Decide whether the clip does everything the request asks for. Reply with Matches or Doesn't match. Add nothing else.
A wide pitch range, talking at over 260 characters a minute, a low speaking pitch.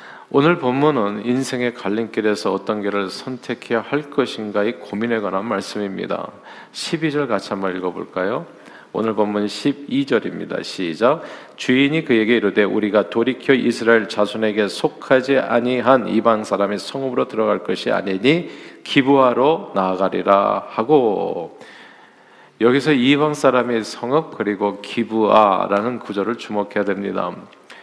Doesn't match